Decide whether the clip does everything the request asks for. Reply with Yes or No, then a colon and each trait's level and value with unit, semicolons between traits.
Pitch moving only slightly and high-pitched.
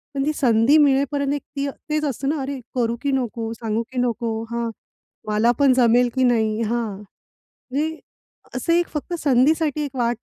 No: average, 3.4 semitones; very high, 255 Hz